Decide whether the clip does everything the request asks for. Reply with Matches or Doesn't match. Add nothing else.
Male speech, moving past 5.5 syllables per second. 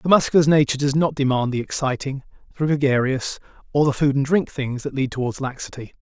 Matches